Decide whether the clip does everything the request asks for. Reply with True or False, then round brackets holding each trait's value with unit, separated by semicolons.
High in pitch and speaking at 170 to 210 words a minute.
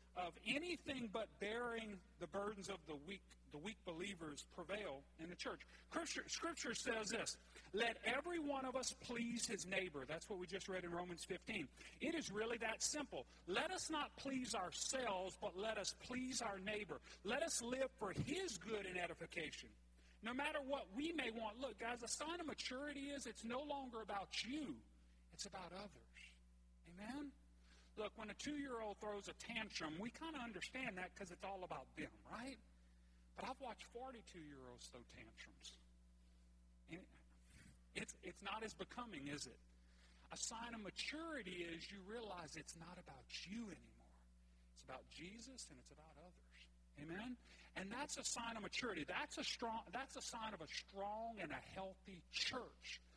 True (205 Hz; 175 wpm)